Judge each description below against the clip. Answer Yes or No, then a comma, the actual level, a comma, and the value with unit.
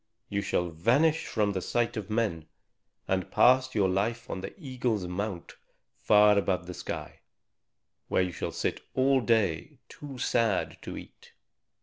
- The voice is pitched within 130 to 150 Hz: No, low, 105 Hz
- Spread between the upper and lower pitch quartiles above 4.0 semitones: Yes, average, 4.6 semitones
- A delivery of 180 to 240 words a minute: No, average, 150 wpm